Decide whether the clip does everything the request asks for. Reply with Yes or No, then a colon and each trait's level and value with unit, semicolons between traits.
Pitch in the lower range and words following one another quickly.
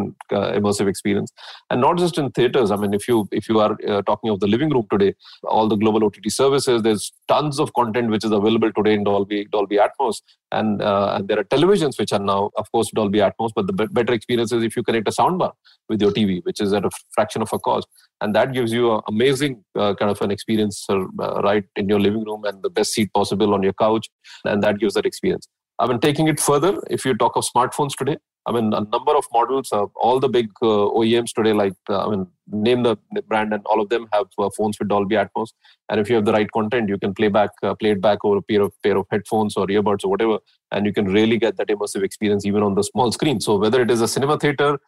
Yes: low, 110 Hz; fast, 255 wpm